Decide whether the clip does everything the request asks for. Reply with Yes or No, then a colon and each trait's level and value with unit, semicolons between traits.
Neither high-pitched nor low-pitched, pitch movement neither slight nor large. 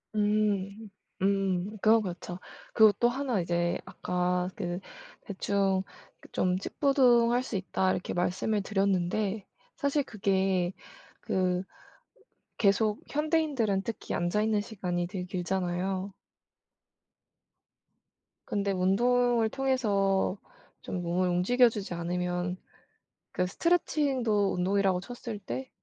No: high, 195 Hz; average, 3.4 semitones